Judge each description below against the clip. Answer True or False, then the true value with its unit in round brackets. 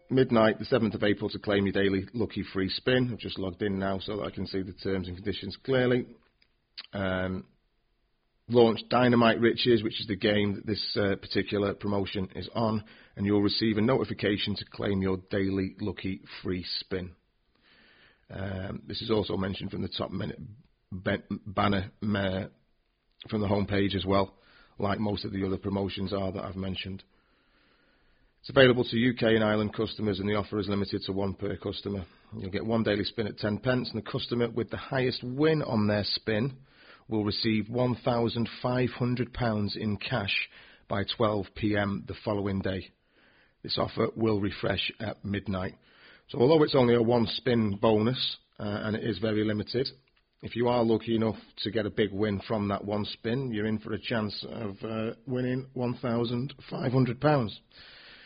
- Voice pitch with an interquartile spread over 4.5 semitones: False (2.9 semitones)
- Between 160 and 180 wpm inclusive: True (175 wpm)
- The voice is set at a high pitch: False (105 Hz)